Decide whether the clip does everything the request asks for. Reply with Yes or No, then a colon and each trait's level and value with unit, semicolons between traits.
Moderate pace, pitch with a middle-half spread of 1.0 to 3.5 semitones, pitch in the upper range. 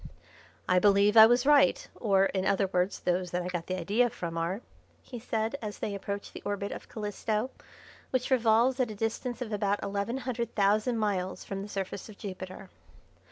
Yes: average, 190 wpm; average, 3.2 semitones; high, 205 Hz